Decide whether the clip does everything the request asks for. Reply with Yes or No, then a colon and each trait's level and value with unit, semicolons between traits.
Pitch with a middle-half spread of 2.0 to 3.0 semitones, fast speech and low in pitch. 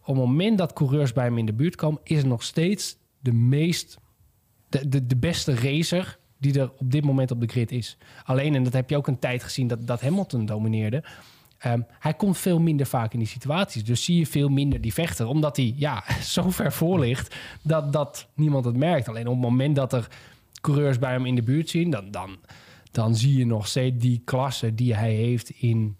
No: average, 3.8 semitones; fast, 225 wpm; low, 130 Hz